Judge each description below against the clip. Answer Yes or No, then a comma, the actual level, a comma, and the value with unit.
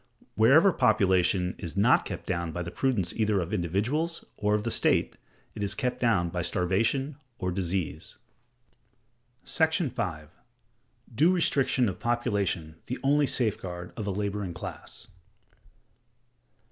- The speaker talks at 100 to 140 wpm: Yes, slow, 135 wpm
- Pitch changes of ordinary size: No, wide, 5.8 semitones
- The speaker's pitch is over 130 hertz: No, low, 105 Hz